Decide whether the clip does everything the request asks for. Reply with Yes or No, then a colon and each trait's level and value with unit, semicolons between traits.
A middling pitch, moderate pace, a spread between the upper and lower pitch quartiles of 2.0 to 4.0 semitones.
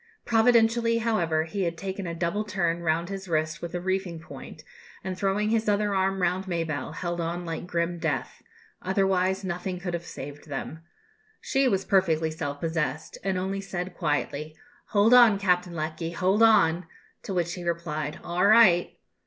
Yes: medium, 180 Hz; average, 170 wpm; average, 3.0 semitones